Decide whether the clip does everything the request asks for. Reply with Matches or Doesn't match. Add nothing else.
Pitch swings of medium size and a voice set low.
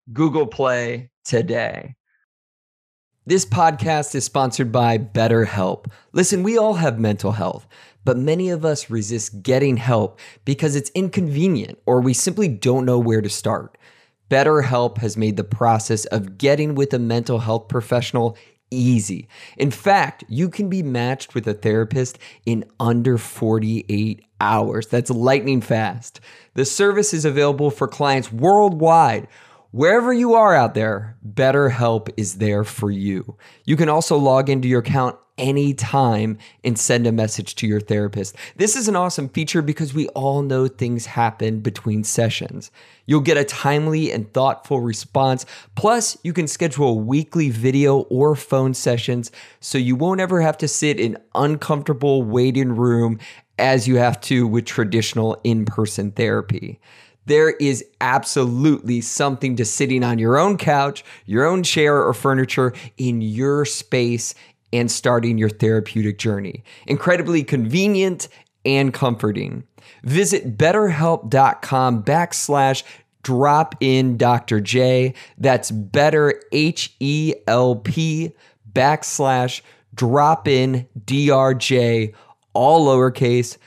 Matches